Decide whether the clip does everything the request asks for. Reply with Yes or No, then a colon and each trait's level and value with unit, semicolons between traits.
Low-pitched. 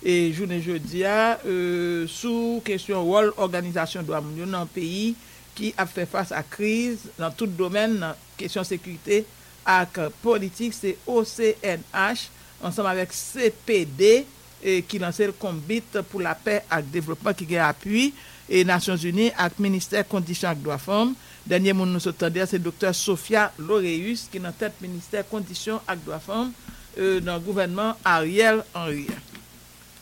No: high, 190 Hz